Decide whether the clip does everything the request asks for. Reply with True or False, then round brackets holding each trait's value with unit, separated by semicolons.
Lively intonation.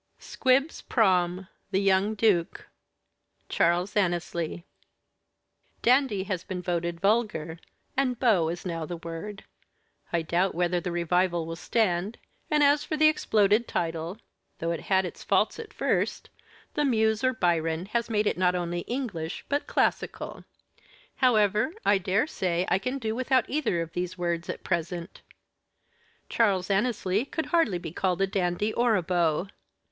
False (4.6 semitones)